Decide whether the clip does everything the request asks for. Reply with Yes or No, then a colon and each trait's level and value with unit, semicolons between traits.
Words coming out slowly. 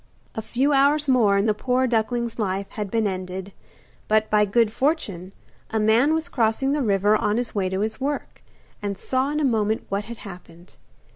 No: average, 195 wpm